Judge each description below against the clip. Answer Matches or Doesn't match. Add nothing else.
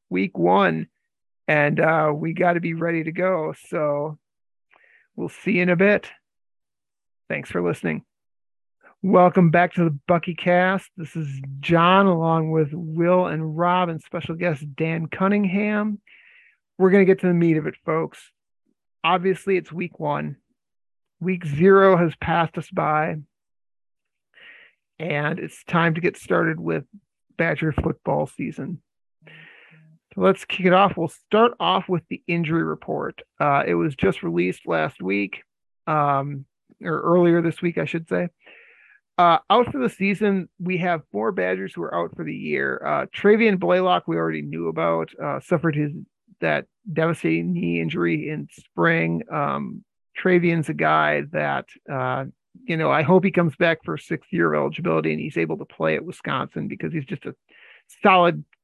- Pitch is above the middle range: Doesn't match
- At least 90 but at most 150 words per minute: Doesn't match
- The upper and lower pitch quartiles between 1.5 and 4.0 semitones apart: Matches